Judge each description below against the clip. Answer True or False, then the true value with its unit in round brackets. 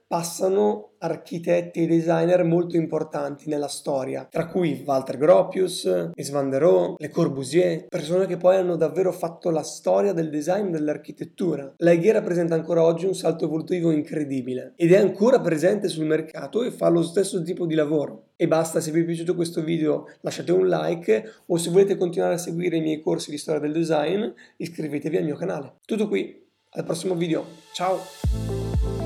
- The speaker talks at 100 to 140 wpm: False (170 wpm)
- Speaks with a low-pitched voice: False (170 Hz)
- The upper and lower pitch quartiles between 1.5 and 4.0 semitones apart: True (2.7 semitones)